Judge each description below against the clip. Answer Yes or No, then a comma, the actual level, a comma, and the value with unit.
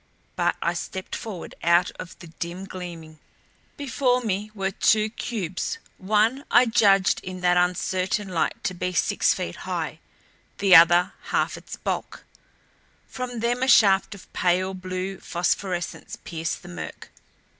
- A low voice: No, medium, 185 Hz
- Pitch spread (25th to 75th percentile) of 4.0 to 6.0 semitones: No, average, 3.3 semitones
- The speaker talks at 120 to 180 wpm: Yes, average, 145 wpm